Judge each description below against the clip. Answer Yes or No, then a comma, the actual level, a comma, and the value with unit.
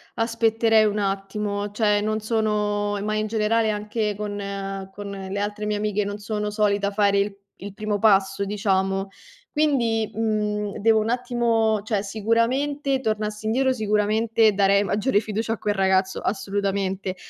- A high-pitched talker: Yes, high, 210 Hz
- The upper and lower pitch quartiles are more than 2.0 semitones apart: No, narrow, 1.7 semitones